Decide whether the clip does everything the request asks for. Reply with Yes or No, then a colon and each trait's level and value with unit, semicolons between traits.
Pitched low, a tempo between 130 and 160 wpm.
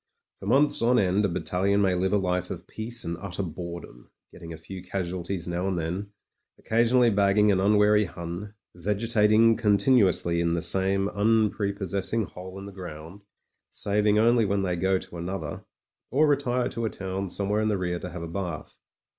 No: low, 100 Hz; average, 190 wpm